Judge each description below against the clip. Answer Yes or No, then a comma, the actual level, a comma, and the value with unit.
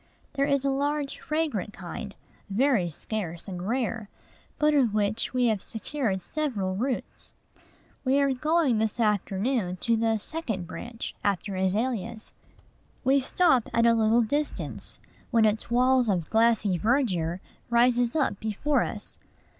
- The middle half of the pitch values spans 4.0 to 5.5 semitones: Yes, average, 4.5 semitones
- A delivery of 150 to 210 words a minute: No, average, 140 wpm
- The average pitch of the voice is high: Yes, high, 230 Hz